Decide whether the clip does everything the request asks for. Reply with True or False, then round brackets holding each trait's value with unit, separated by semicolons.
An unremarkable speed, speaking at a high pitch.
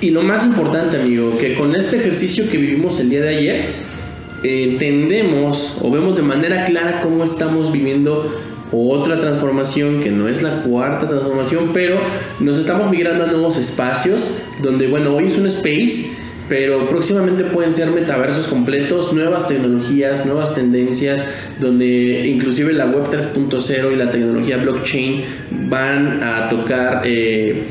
False (150 wpm; 140 Hz)